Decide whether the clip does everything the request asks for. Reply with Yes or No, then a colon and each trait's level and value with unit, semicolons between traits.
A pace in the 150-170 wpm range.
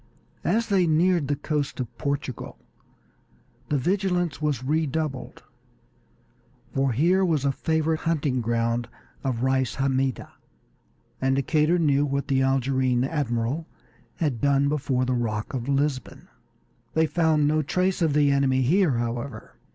No: slow, 135 wpm